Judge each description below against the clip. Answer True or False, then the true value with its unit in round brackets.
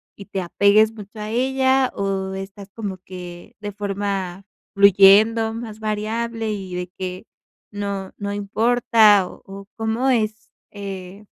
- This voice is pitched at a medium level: False (205 Hz)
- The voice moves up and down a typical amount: False (2.3 semitones)